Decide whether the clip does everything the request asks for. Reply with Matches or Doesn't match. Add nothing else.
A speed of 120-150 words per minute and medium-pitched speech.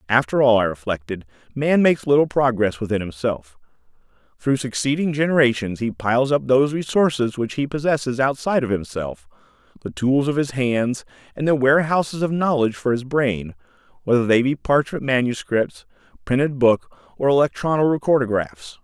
Doesn't match